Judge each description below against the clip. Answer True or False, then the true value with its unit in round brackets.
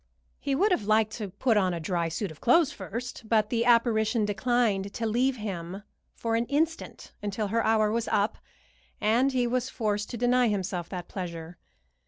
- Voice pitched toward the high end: True (220 Hz)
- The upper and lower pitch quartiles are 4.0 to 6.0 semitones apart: False (3.4 semitones)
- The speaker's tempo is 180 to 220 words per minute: True (185 wpm)